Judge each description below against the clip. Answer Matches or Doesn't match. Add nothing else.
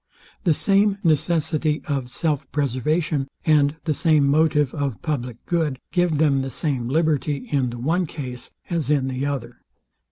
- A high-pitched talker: Doesn't match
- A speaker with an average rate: Matches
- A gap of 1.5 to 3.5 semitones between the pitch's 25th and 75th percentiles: Matches